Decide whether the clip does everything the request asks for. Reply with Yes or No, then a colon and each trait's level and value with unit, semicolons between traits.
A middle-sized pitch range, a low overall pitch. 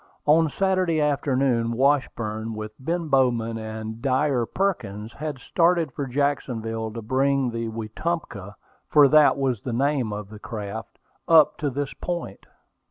Yes: average, 4.8 semitones; low, 130 Hz